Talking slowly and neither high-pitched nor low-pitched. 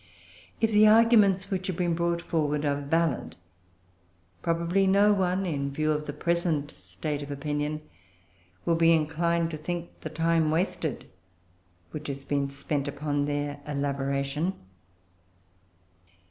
Yes: slow, 130 wpm; medium, 155 Hz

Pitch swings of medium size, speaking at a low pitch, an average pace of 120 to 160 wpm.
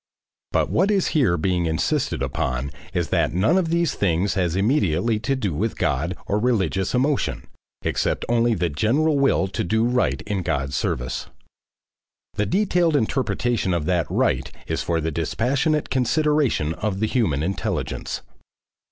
No: wide, 7.9 semitones; low, 105 Hz; average, 150 wpm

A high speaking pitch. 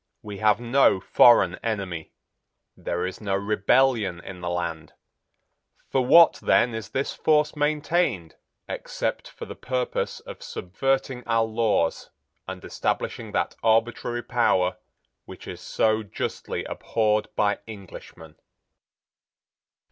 No: low, 110 Hz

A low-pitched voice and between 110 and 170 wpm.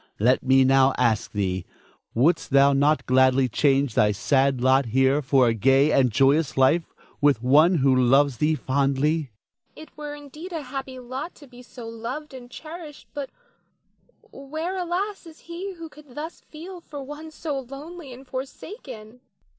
No: medium, 175 Hz; average, 165 wpm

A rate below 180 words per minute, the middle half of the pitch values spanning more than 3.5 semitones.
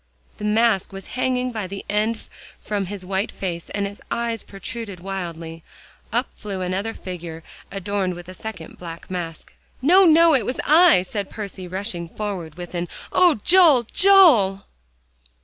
Yes: average, 155 wpm; average, 4.4 semitones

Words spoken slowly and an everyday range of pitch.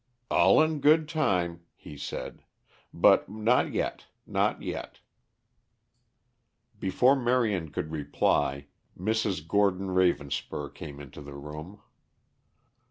No: slow, 100 wpm; wide, 6.9 semitones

